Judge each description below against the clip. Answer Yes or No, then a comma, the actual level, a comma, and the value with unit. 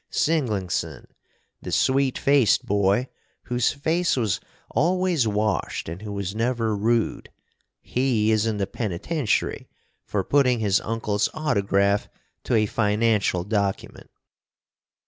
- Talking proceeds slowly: Yes, slow, 115 wpm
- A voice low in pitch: Yes, low, 110 Hz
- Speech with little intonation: No, average, 4.0 semitones